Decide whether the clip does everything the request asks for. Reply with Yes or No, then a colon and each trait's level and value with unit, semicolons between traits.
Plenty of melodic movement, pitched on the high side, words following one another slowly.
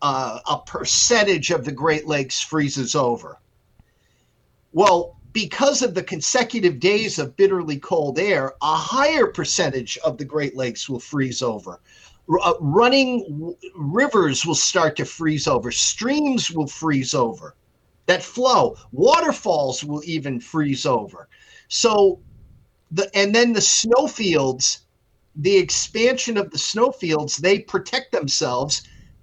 No: wide, 7.0 semitones; medium, 165 Hz; slow, 130 wpm